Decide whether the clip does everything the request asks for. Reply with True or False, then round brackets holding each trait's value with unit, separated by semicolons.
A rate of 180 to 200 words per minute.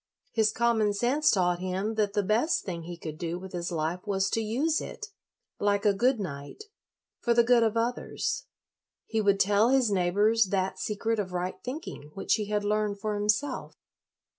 True (185 wpm)